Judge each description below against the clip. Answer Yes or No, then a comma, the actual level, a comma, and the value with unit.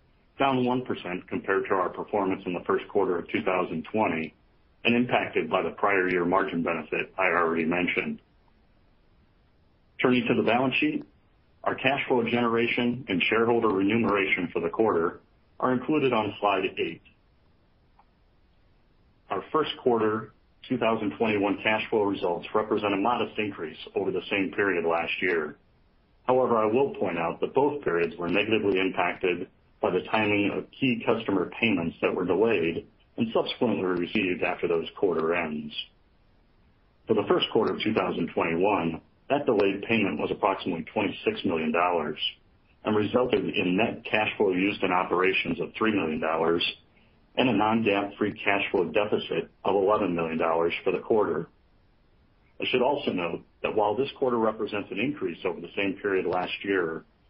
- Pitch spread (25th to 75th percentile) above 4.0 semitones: Yes, average, 5.2 semitones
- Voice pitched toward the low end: Yes, low, 100 Hz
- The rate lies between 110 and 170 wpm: Yes, average, 150 wpm